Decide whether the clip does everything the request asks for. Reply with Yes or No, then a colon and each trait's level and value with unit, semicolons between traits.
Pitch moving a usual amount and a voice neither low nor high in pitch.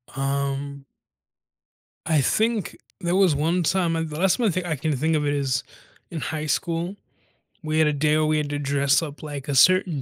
Yes: average, 3.3 semitones; medium, 155 Hz